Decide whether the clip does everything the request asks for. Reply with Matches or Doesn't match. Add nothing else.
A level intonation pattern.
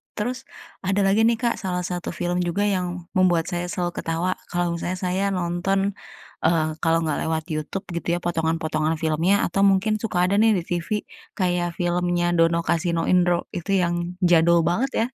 Matches